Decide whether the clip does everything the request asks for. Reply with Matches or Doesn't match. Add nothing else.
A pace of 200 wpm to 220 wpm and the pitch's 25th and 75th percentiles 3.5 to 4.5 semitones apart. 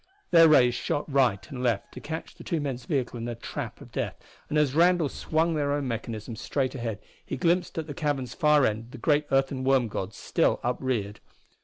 Matches